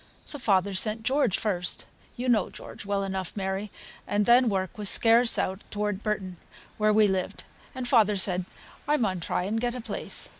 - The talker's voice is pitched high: Yes, high, 210 Hz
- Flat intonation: No, average, 3.2 semitones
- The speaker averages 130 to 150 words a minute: No, average, 185 wpm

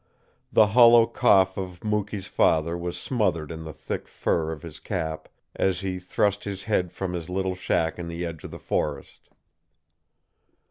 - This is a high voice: No, very low, 90 Hz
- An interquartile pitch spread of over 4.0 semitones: No, average, 3.2 semitones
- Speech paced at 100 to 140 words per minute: No, average, 170 wpm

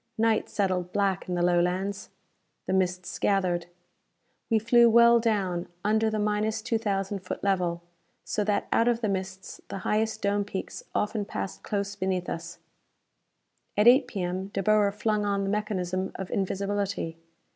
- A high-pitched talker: Yes, high, 200 Hz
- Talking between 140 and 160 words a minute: Yes, average, 155 wpm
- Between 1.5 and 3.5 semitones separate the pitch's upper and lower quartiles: Yes, narrow, 2.6 semitones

